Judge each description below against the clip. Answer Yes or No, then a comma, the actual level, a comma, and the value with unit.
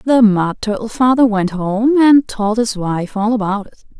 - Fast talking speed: No, average, 195 wpm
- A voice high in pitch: Yes, high, 220 Hz